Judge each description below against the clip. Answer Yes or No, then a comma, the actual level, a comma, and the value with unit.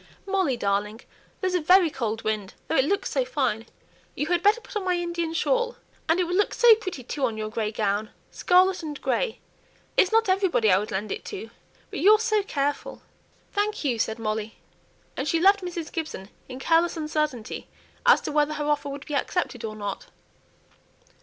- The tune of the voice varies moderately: No, wide, 8.8 semitones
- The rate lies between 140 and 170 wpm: No, average, 190 wpm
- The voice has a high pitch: Yes, very high, 305 Hz